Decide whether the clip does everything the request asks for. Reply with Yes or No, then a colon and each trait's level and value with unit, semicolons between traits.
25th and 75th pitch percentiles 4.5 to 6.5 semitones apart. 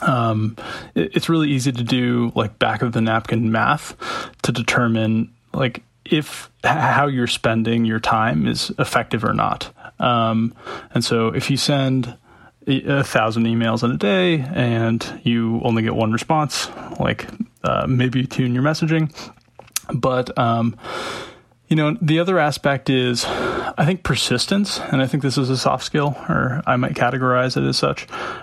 No: average, 3.9 semitones